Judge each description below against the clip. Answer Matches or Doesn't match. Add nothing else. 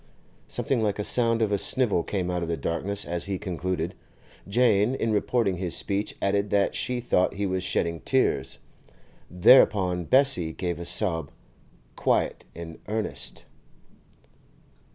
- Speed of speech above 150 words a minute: Doesn't match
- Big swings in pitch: Doesn't match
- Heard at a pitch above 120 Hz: Doesn't match